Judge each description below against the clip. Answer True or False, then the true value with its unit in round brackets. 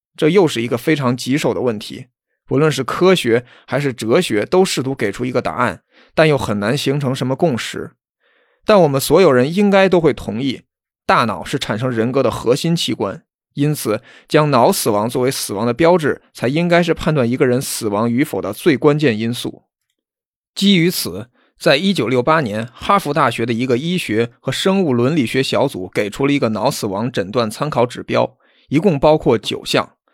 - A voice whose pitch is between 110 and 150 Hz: True (135 Hz)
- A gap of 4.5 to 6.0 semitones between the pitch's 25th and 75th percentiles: True (5.1 semitones)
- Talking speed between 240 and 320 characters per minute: True (275 characters per minute)